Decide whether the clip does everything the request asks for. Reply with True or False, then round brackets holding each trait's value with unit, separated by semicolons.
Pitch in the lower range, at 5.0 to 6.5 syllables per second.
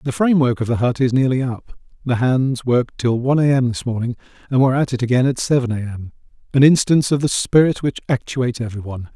True (125 Hz; 6.3 syllables/s)